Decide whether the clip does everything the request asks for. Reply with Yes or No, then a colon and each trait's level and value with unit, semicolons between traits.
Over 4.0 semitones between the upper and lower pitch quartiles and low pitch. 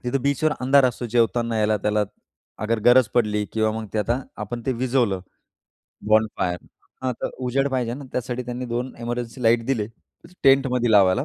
No: average, 2.7 semitones; low, 120 Hz